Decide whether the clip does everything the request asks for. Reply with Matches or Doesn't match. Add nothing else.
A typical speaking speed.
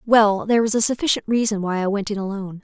Doesn't match